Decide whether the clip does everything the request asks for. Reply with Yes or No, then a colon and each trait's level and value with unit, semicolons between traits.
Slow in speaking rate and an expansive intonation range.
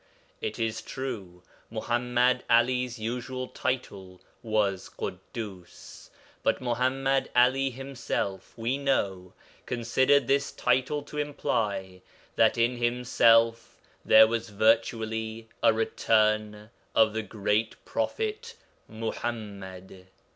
No: slow, 95 wpm; average, 2.9 semitones